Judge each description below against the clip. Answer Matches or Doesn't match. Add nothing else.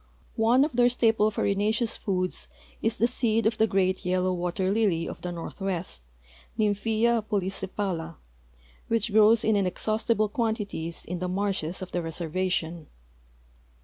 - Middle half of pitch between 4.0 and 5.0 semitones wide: Doesn't match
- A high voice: Matches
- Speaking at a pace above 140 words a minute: Doesn't match